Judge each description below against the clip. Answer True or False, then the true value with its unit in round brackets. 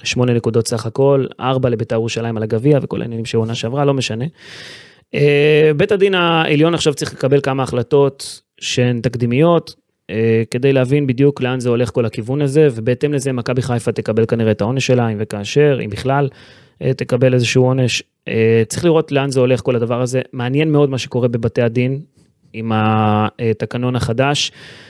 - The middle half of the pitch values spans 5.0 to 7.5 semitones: False (3.4 semitones)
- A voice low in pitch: True (125 Hz)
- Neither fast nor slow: False (165 wpm)